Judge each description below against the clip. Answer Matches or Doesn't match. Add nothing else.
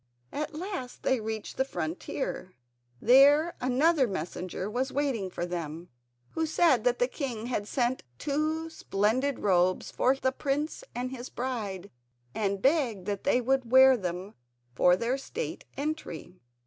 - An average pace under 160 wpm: Matches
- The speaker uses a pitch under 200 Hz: Doesn't match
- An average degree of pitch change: Doesn't match